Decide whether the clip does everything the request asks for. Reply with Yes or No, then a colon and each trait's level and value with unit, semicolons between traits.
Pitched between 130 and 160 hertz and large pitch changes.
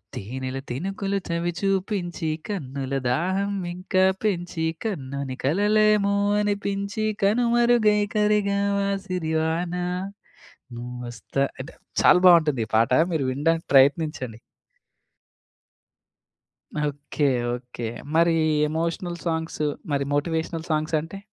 No: medium, 170 Hz; wide, 6.0 semitones